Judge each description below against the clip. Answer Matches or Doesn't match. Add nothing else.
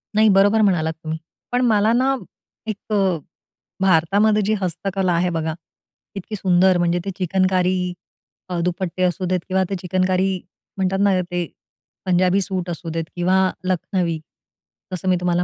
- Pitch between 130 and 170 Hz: Doesn't match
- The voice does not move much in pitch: Matches